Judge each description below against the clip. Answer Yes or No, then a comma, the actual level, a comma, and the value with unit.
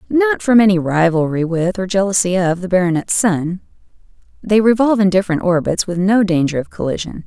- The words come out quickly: No, average, 175 wpm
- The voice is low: No, high, 190 Hz